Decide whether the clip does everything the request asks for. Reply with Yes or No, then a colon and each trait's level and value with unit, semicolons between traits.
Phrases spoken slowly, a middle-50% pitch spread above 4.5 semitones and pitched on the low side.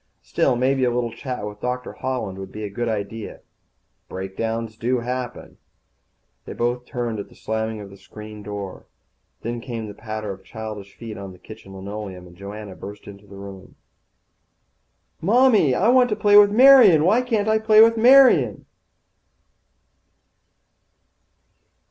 No: average, 155 wpm; average, 5.2 semitones; low, 115 Hz